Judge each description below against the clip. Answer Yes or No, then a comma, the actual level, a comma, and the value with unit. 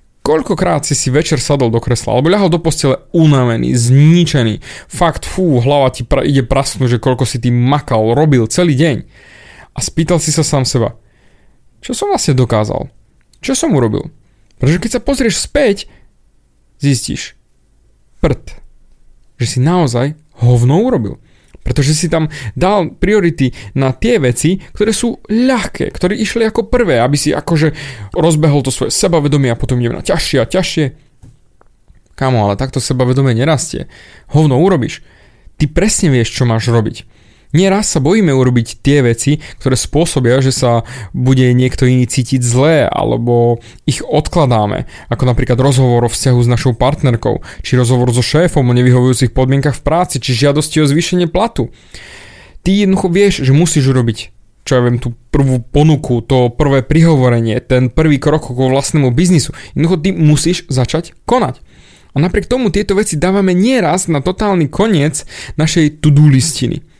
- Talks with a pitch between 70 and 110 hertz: No, medium, 140 Hz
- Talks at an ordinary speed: Yes, average, 155 wpm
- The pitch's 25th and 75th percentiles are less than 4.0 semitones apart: No, average, 4.7 semitones